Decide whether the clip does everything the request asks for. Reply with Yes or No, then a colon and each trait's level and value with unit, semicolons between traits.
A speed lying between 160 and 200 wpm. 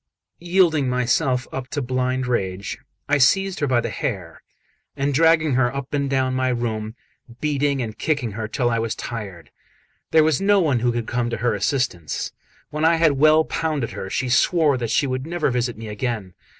Yes: average, 190 wpm